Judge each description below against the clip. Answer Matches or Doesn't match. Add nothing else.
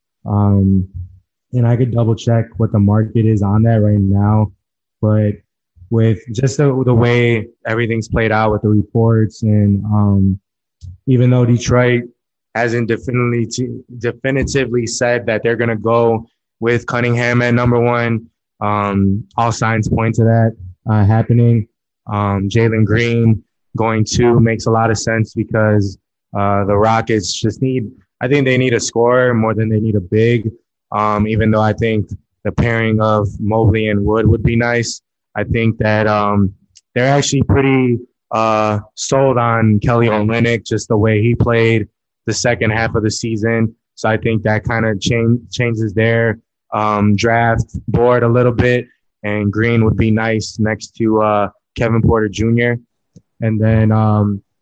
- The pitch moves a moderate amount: Doesn't match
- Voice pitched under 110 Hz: Doesn't match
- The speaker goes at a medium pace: Matches